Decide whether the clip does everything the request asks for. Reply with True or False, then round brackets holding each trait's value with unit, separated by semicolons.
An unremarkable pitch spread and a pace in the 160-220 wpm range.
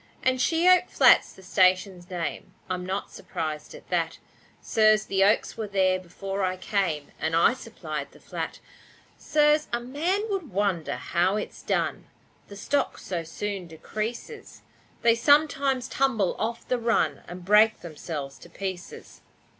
False (5.0 semitones; 150 wpm)